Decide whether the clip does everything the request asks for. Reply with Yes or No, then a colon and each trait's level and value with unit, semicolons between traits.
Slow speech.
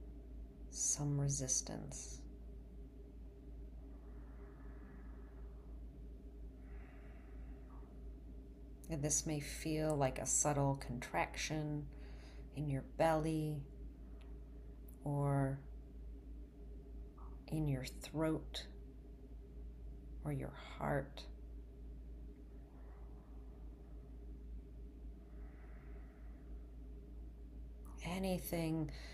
Yes: slow, 45 wpm